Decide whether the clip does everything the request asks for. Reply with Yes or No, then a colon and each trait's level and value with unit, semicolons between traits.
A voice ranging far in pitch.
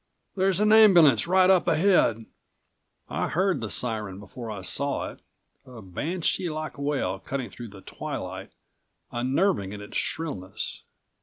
Yes: wide, 8.9 semitones